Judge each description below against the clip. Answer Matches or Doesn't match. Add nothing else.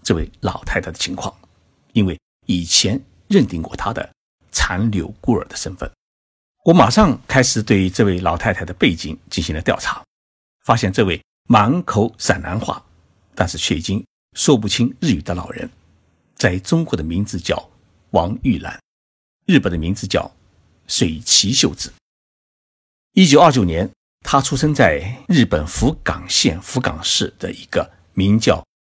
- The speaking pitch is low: Matches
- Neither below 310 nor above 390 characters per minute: Doesn't match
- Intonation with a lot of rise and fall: Doesn't match